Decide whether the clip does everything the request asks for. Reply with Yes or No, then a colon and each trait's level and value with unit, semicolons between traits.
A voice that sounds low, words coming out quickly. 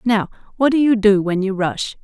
No: high, 210 Hz; fast, 235 wpm